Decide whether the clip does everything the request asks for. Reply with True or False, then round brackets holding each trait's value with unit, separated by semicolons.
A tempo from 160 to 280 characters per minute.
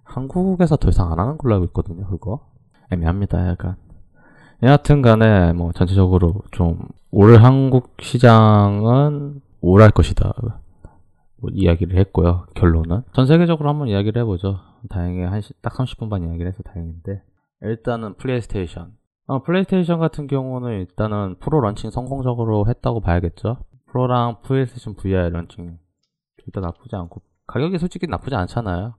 False (350 characters per minute)